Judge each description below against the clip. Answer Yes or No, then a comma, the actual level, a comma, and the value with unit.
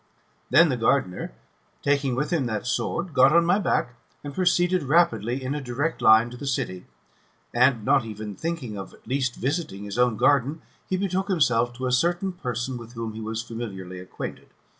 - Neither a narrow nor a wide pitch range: No, wide, 5.7 semitones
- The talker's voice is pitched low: Yes, low, 130 Hz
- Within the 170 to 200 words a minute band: Yes, average, 185 wpm